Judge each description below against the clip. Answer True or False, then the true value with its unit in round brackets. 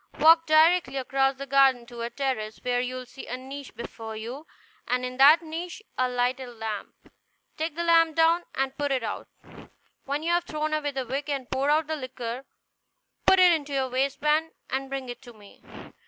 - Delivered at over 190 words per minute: True (200 wpm)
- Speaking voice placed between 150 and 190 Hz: False (270 Hz)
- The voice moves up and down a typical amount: True (3.6 semitones)